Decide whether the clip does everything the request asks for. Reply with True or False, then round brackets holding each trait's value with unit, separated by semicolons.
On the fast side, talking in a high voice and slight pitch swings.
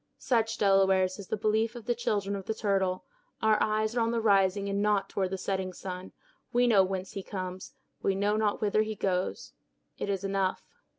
True (210 wpm; 200 Hz; 2.2 semitones)